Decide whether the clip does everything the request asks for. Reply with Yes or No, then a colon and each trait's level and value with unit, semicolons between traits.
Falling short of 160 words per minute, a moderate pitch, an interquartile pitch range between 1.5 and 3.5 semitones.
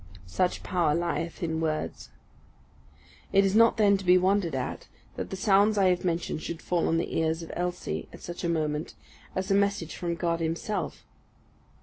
No: average, 185 wpm; medium, 175 Hz; average, 2.8 semitones